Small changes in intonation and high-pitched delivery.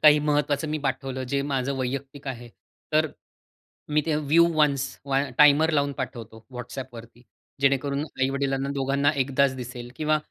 No: narrow, 2.2 semitones; medium, 140 Hz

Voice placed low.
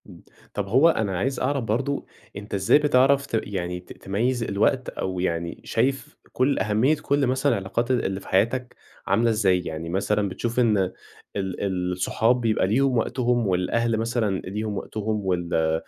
Yes: low, 110 Hz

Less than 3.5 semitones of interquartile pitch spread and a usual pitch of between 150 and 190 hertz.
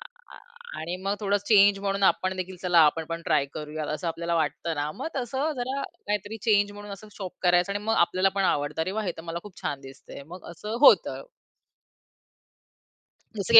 No: average, 3.8 semitones; medium, 185 Hz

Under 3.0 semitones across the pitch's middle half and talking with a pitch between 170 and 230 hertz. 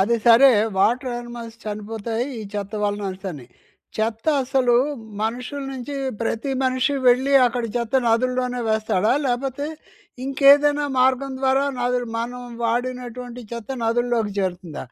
No: narrow, 2.5 semitones; high, 245 Hz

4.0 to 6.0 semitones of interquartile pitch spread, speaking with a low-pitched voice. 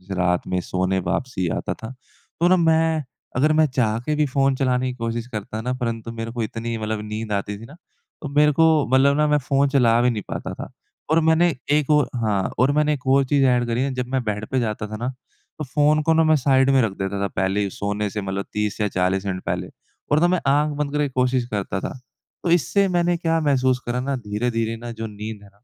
Yes: wide, 5.5 semitones; low, 125 Hz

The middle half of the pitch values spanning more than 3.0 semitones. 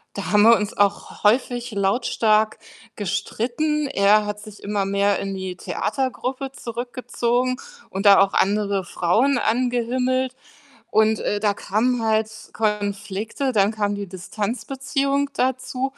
Yes: average, 3.8 semitones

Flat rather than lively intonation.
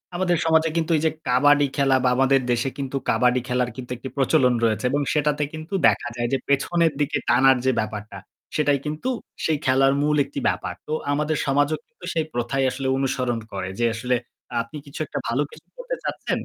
No: average, 3.2 semitones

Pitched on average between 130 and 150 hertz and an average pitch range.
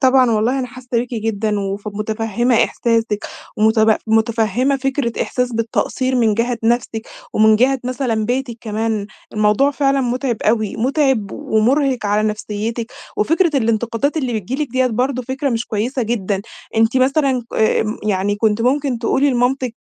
No: high, 235 Hz; average, 3.0 semitones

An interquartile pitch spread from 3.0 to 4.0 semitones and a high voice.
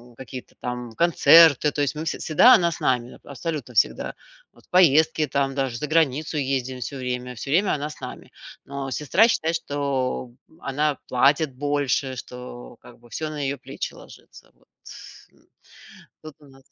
No: average, 3.3 semitones; medium, 140 Hz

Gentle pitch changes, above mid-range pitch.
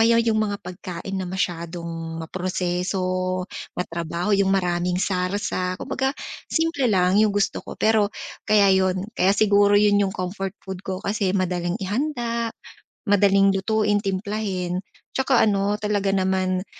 Yes: narrow, 2.2 semitones; high, 195 Hz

